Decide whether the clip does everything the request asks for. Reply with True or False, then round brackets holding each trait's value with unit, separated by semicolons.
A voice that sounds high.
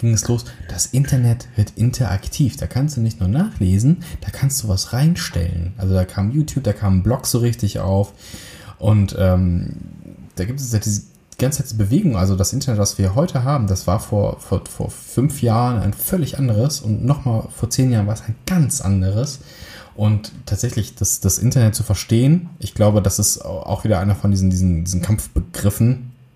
False (110 Hz)